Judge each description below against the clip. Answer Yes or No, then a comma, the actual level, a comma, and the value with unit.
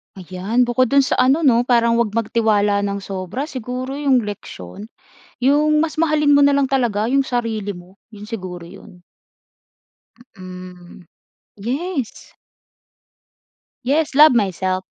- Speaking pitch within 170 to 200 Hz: No, high, 235 Hz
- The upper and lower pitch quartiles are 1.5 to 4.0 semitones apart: No, wide, 5.5 semitones